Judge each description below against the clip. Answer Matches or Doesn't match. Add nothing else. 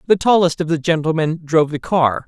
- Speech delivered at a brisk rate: Matches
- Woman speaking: Doesn't match